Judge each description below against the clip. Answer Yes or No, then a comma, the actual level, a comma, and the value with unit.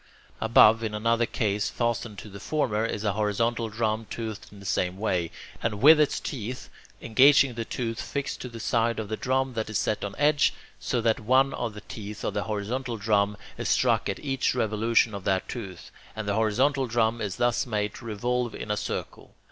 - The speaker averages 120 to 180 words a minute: No, fast, 205 wpm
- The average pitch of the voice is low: Yes, low, 110 Hz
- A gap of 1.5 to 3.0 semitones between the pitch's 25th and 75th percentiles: Yes, narrow, 2.4 semitones